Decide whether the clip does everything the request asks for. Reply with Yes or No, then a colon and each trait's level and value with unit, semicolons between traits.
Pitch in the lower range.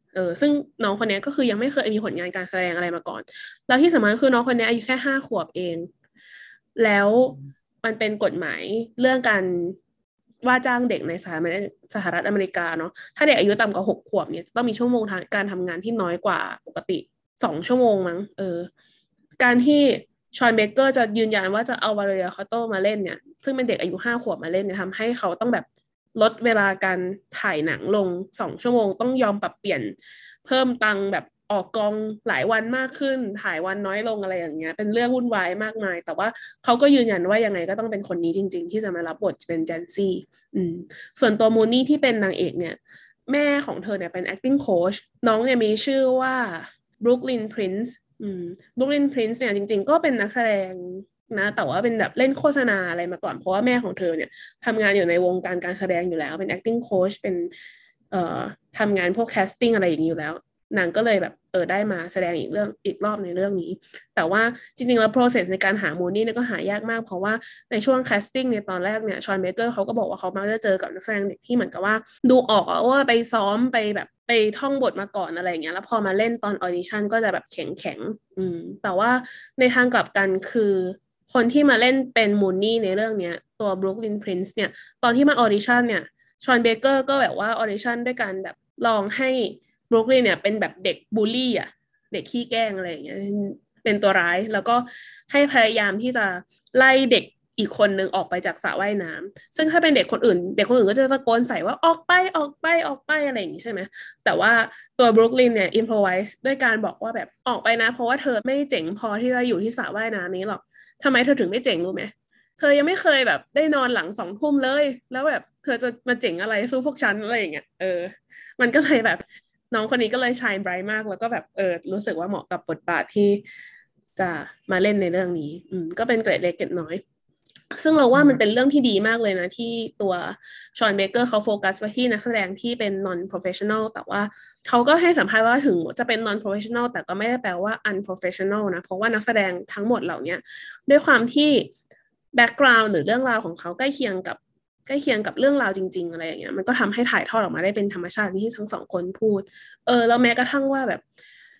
No: high, 220 Hz